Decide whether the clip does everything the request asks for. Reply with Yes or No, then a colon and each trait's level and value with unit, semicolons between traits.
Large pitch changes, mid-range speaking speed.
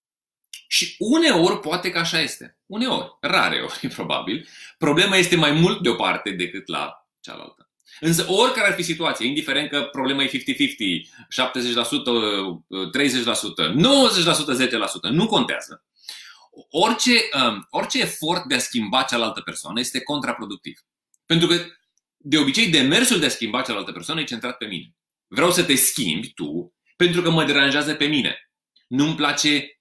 Yes: wide, 6.0 semitones; average, 145 wpm